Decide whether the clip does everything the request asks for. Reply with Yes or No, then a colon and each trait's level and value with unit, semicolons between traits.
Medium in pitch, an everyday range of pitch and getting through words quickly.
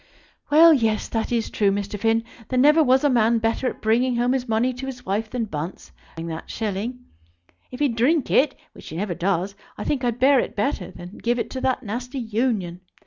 No: high, 235 Hz; average, 3.8 semitones; fast, 215 wpm